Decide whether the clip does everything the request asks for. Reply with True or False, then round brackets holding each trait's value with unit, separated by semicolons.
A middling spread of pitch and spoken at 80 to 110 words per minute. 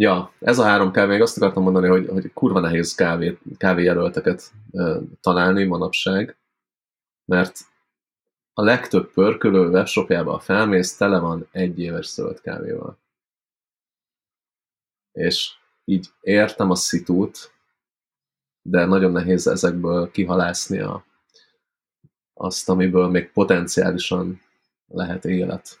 False (0.9 semitones; 105 wpm)